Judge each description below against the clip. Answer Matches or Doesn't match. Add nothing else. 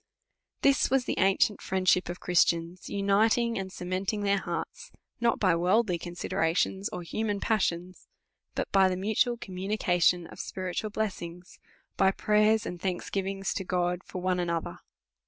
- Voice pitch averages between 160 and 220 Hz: Matches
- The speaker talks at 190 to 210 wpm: Doesn't match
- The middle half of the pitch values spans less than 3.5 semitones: Matches